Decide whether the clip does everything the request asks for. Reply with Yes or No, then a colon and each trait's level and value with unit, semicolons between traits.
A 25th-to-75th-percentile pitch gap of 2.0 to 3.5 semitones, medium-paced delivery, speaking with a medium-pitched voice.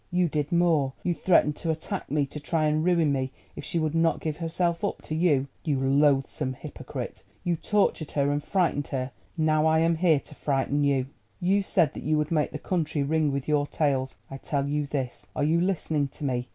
No: average, 2.8 semitones; fast, 210 wpm; medium, 150 Hz